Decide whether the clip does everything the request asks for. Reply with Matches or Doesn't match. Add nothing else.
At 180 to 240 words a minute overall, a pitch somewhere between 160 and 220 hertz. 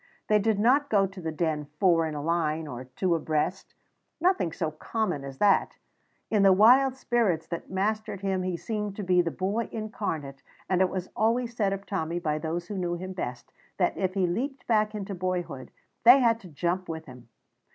Matches